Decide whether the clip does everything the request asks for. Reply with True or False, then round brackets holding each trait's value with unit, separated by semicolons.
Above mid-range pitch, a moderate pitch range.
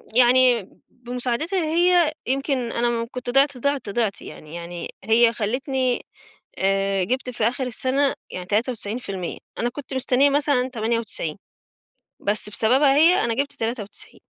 True (245 Hz; 3.7 semitones)